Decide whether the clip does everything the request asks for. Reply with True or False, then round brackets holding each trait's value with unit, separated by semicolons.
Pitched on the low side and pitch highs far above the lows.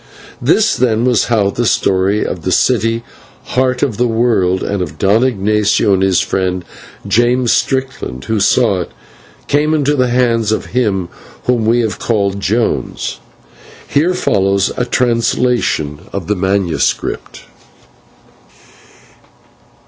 False (110 Hz; 4.2 semitones)